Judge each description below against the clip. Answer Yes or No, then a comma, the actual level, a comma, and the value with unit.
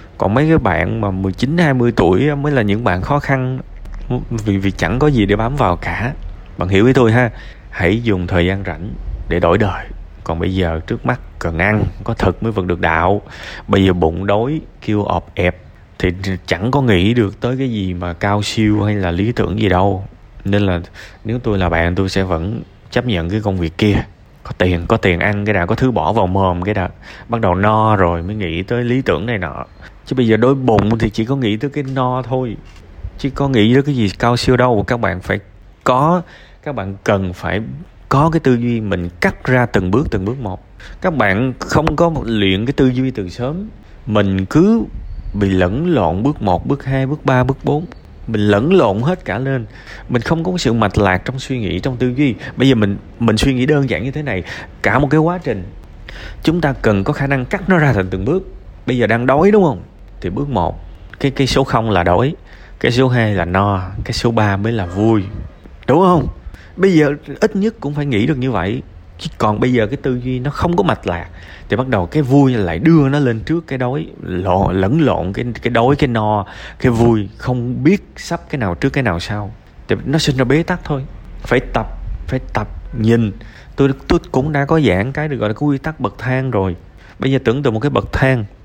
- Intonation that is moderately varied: No, wide, 5.7 semitones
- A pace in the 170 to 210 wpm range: No, average, 230 wpm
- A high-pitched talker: No, low, 110 Hz